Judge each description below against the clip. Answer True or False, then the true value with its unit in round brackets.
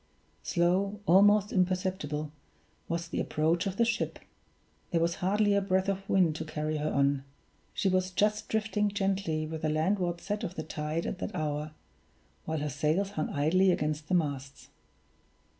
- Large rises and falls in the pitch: False (4.2 semitones)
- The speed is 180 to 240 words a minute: False (165 wpm)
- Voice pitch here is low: False (175 Hz)